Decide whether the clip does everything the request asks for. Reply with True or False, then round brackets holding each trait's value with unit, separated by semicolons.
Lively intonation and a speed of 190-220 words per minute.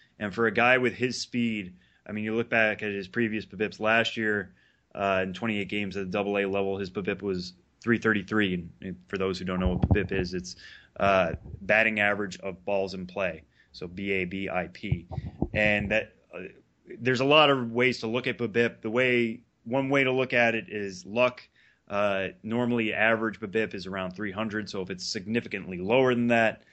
False (3.2 semitones; 195 wpm)